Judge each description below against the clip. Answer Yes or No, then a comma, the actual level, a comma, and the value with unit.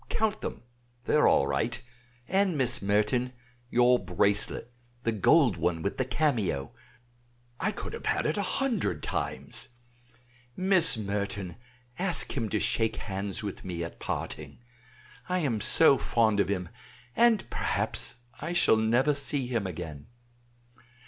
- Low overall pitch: Yes, low, 115 Hz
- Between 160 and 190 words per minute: No, average, 140 wpm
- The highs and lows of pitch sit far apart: Yes, wide, 7.0 semitones